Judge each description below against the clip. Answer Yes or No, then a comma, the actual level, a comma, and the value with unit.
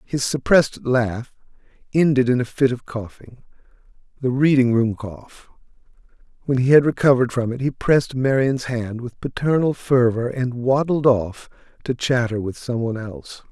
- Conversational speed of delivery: Yes, average, 145 wpm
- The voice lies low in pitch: Yes, low, 125 Hz